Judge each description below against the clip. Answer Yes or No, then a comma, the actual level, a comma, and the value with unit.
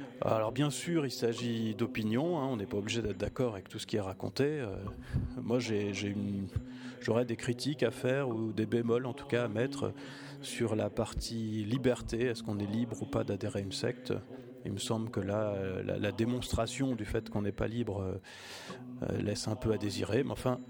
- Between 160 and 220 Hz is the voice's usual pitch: No, low, 115 Hz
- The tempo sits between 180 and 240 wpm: Yes, average, 210 wpm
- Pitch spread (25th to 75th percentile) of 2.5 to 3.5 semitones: Yes, average, 3.0 semitones